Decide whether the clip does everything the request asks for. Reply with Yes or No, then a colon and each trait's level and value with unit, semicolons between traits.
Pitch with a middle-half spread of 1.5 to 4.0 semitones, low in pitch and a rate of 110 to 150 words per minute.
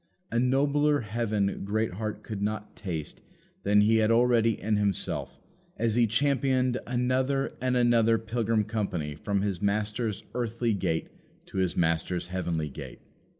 Yes: average, 3.3 semitones; low, 110 Hz; average, 140 wpm